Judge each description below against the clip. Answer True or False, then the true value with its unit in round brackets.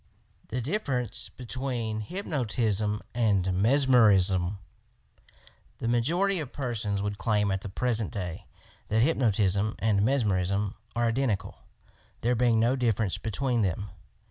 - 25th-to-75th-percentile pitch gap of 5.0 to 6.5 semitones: False (3.8 semitones)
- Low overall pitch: True (110 Hz)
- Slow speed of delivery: True (115 wpm)